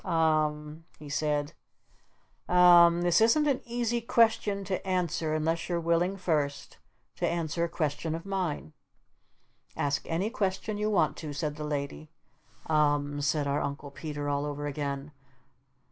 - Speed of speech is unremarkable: Yes, average, 165 wpm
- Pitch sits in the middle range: Yes, medium, 160 Hz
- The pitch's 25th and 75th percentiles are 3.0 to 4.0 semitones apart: Yes, average, 3.6 semitones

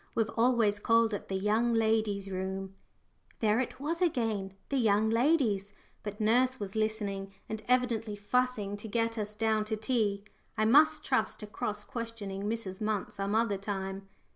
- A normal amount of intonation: No, narrow, 2.3 semitones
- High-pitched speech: Yes, high, 215 Hz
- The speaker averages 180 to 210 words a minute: No, average, 165 wpm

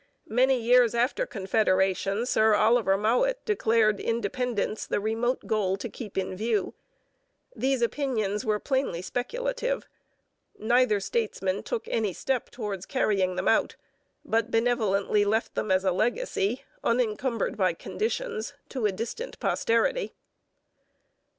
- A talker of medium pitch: No, high, 225 Hz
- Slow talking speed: Yes, slow, 125 wpm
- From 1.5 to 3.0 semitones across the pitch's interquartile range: No, average, 3.7 semitones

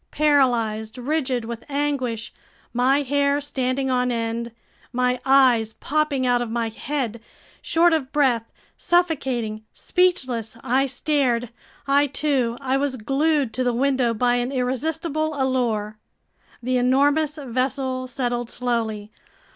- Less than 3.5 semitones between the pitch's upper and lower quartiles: Yes, average, 3.0 semitones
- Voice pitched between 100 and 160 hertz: No, very high, 255 Hz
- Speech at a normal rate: No, slow, 120 wpm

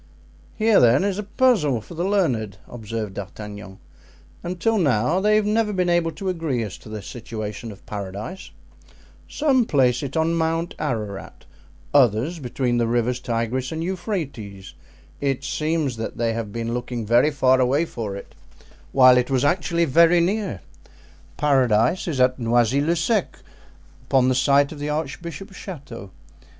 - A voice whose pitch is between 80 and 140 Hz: Yes, low, 135 Hz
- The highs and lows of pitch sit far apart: Yes, wide, 6.7 semitones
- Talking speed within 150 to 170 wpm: Yes, average, 155 wpm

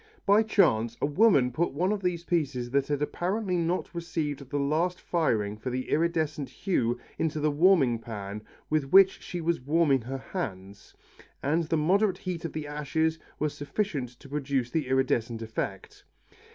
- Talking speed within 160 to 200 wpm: Yes, average, 165 wpm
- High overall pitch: No, medium, 150 Hz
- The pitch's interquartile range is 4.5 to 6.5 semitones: Yes, average, 5.0 semitones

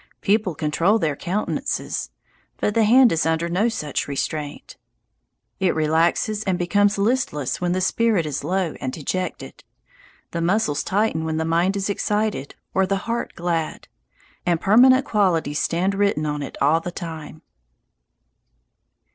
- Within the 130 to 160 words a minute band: Yes, average, 145 wpm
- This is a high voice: No, medium, 175 Hz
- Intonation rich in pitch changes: No, average, 4.4 semitones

